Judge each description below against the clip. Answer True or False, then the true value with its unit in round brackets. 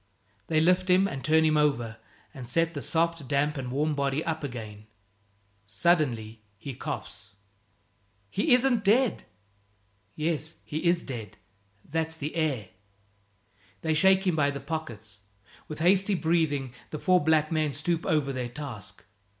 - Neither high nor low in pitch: True (155 Hz)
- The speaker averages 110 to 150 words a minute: True (145 wpm)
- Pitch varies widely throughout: False (3.9 semitones)